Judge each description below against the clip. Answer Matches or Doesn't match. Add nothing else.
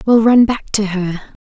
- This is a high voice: Matches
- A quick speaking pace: Matches